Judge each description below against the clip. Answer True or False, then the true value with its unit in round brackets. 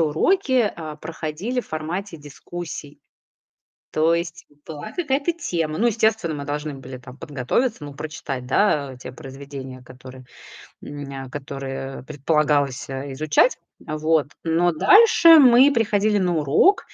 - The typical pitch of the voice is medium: True (155 Hz)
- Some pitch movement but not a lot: False (6.6 semitones)